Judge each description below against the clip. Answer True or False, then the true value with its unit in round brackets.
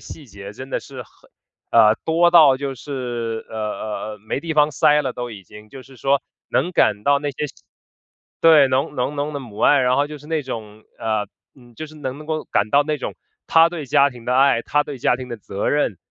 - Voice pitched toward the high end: False (135 Hz)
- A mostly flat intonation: False (4.3 semitones)